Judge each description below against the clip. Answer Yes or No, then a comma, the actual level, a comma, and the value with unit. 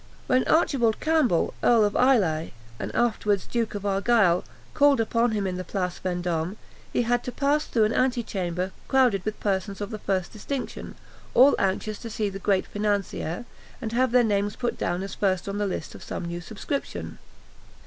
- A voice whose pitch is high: Yes, high, 210 Hz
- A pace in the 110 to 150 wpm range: No, average, 185 wpm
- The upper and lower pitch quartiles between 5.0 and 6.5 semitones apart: No, average, 4.1 semitones